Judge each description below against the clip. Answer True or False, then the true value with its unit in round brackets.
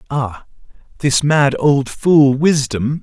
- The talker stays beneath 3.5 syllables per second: True (3.1 syllables/s)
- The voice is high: False (140 Hz)